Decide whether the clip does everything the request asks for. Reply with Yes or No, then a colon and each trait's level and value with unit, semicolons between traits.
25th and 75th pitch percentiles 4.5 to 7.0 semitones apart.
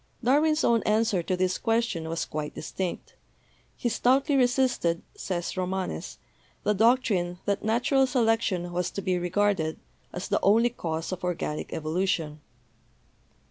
Yes: average, 5.1 semitones